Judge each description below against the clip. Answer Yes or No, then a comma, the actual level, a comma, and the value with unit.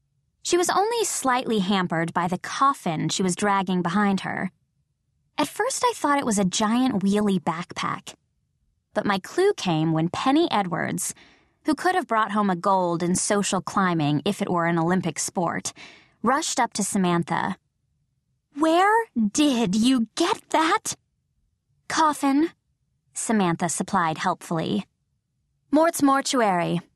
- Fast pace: No, slow, 135 wpm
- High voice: Yes, high, 205 Hz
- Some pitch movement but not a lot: No, wide, 7.7 semitones